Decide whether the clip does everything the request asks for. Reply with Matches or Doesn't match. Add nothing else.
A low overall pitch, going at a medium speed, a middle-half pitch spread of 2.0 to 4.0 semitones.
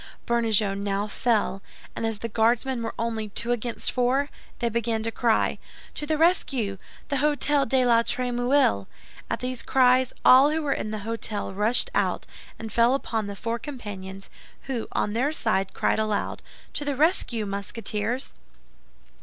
Doesn't match